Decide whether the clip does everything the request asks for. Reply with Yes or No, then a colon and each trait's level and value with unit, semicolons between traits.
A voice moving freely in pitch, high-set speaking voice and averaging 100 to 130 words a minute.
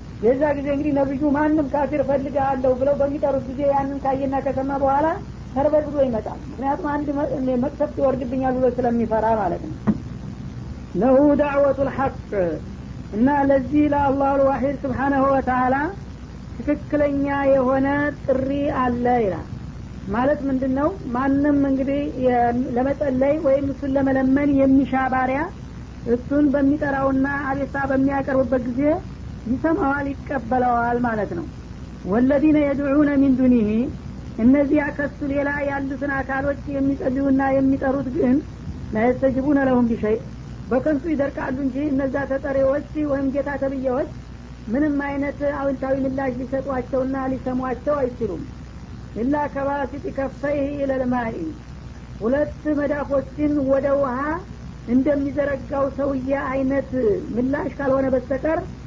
No: narrow, 1.3 semitones; very high, 275 Hz; average, 105 wpm